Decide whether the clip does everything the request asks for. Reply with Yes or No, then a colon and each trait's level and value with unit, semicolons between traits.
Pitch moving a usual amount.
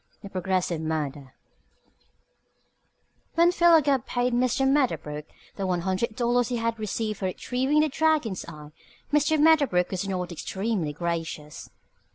No: wide, 7.5 semitones